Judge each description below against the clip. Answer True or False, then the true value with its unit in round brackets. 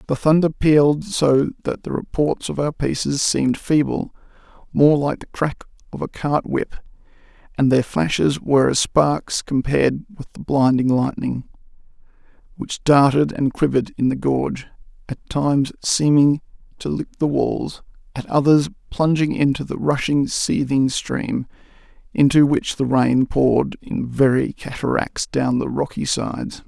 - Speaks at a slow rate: False (145 wpm)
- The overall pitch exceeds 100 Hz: True (140 Hz)